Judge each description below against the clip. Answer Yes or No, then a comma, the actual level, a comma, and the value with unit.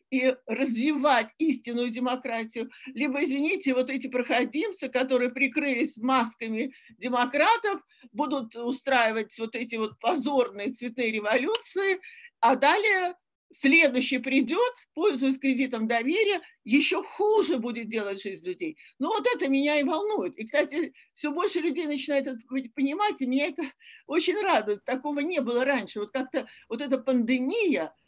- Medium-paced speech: Yes, average, 135 wpm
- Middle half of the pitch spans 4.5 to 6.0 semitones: Yes, average, 5.2 semitones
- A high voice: Yes, very high, 275 Hz